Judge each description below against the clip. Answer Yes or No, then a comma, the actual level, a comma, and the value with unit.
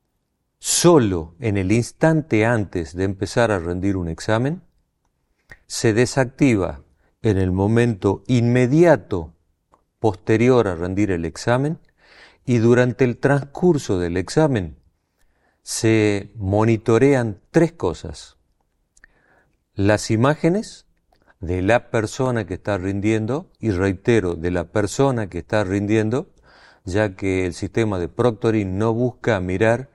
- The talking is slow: Yes, slow, 115 wpm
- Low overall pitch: Yes, low, 110 Hz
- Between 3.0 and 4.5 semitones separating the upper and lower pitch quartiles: No, average, 4.9 semitones